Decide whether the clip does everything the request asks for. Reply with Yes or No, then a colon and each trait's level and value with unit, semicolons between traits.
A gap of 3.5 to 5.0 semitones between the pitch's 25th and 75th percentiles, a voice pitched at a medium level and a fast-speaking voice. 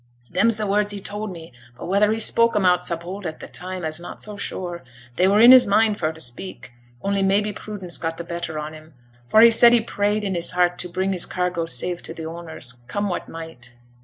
Yes: average, 3.9 semitones; medium, 180 Hz; fast, 240 wpm